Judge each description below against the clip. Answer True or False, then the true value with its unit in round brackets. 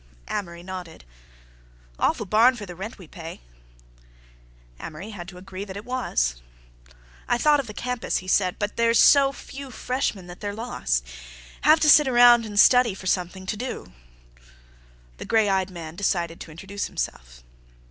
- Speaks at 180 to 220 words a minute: False (170 wpm)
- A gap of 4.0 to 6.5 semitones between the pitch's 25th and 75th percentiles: True (5.3 semitones)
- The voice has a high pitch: True (200 Hz)